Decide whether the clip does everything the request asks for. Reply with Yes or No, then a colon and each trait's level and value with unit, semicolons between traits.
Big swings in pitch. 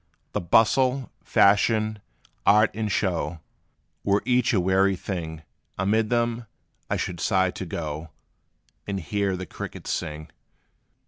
No: average, 3.6 semitones